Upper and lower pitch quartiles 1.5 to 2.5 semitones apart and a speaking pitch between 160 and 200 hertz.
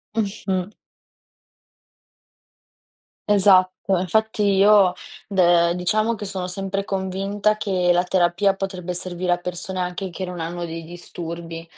Yes: narrow, 2.0 semitones; medium, 185 Hz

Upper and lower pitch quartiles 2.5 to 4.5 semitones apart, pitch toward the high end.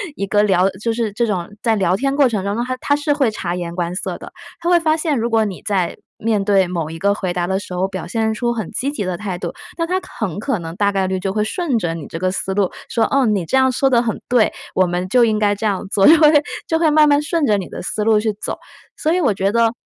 No: average, 5.2 semitones; high, 215 Hz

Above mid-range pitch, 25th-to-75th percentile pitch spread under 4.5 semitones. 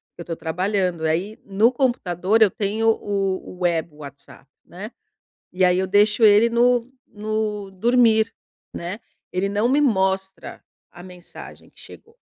Yes: high, 200 Hz; average, 3.5 semitones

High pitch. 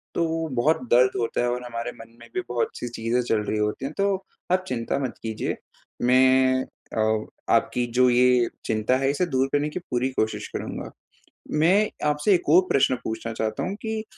No: low, 125 Hz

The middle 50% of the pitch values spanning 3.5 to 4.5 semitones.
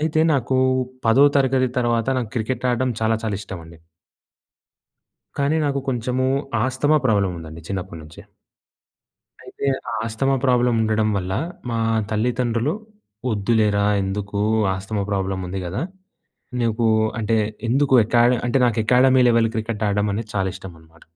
Yes: average, 3.9 semitones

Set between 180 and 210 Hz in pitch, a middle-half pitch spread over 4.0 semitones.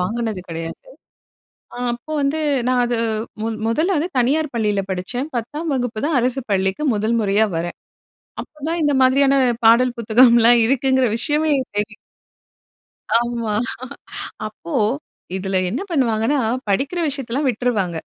No: high, 240 Hz; average, 4.4 semitones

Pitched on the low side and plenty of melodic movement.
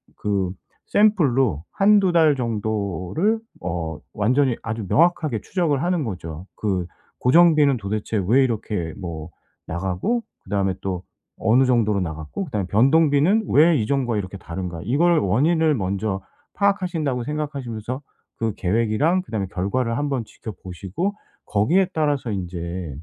Yes: low, 115 Hz; wide, 7.9 semitones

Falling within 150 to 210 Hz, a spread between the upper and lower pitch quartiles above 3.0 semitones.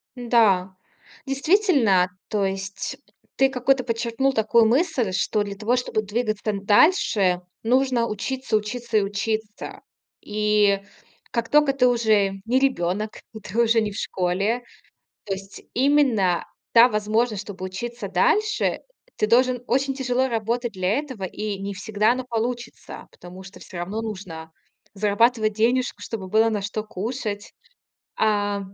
No: high, 220 Hz; average, 3.5 semitones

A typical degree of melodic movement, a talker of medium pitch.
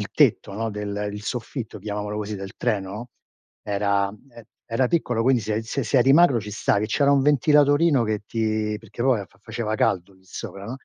No: average, 3.2 semitones; low, 110 Hz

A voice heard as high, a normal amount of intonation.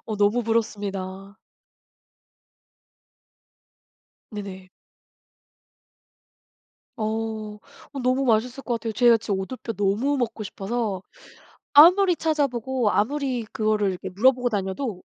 Yes: high, 225 Hz; average, 3.7 semitones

